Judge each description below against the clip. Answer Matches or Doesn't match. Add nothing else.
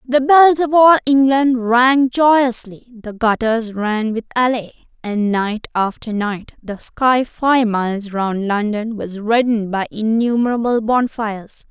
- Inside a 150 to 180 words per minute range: Doesn't match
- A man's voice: Doesn't match